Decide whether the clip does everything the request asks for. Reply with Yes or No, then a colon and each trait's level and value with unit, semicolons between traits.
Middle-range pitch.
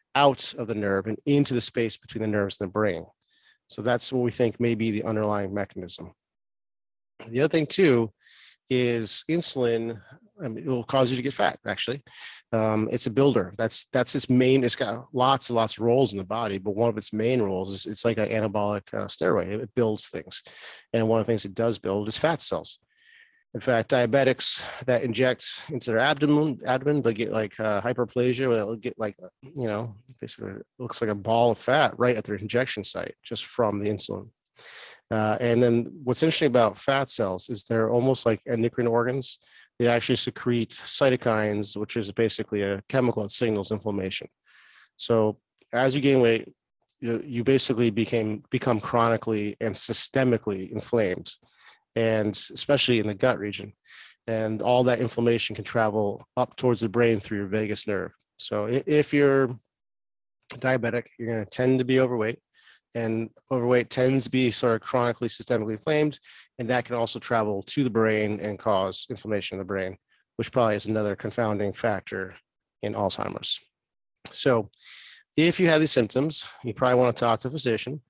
No: low, 115 Hz